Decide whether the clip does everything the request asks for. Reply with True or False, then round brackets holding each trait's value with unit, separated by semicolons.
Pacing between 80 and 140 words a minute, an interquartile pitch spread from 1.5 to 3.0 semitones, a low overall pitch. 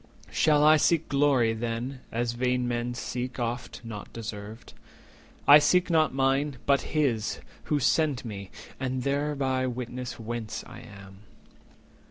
False (135 wpm; 3.5 semitones; 125 Hz)